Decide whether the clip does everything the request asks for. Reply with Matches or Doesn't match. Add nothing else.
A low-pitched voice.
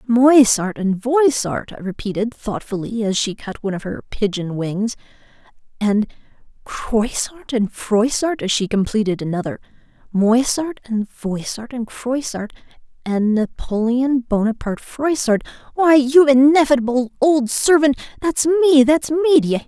Doesn't match